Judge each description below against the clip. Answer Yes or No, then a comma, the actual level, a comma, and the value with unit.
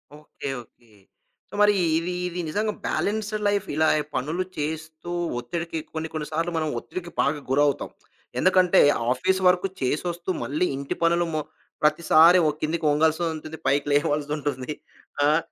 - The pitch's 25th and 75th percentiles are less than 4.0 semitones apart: Yes, average, 2.9 semitones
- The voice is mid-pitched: Yes, medium, 160 Hz